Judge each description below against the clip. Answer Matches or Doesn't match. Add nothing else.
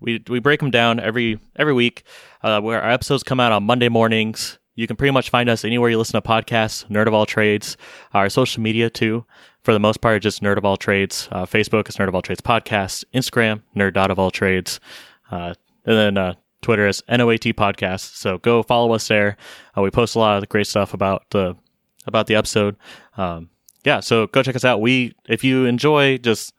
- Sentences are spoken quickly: Matches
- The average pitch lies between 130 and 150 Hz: Doesn't match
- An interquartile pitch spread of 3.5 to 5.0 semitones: Doesn't match